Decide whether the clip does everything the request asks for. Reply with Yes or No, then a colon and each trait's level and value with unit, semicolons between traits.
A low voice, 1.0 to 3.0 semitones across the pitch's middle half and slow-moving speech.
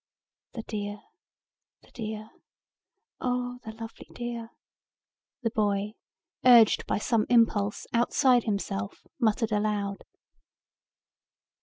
No: high, 220 Hz; narrow, 2.4 semitones; slow, 95 wpm